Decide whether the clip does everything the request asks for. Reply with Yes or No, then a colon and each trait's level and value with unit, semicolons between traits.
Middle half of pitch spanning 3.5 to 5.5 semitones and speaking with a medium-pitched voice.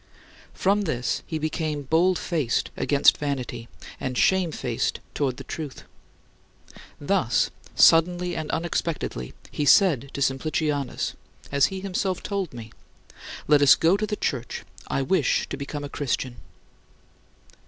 Yes: average, 4.4 semitones; medium, 150 Hz